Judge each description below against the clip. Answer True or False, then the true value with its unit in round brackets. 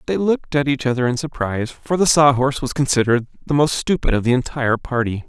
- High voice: False (130 Hz)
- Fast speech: True (225 wpm)